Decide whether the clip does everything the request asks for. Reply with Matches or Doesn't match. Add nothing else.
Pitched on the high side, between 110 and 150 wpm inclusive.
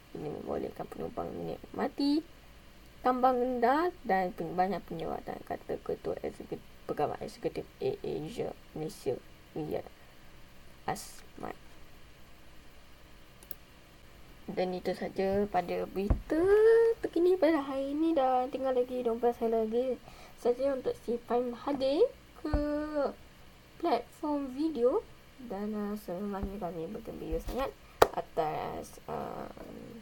Doesn't match